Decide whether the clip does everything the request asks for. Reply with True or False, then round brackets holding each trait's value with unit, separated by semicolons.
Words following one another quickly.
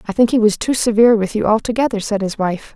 True (260 wpm)